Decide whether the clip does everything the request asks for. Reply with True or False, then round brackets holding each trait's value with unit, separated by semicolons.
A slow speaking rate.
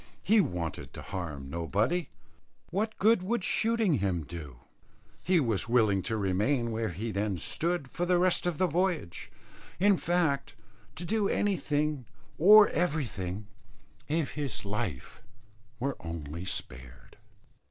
True (130 wpm)